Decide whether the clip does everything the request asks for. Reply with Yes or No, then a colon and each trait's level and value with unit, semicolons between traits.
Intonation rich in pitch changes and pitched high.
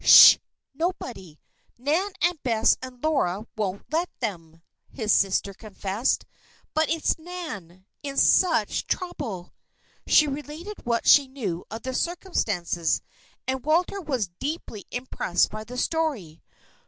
Yes: wide, 7.9 semitones; very high, 255 Hz